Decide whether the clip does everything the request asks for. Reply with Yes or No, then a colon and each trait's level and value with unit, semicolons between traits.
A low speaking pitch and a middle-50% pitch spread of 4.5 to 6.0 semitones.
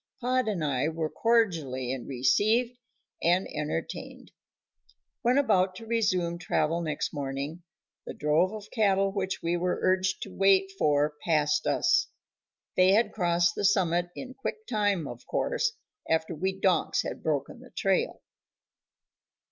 No: medium, 185 Hz; average, 4.8 semitones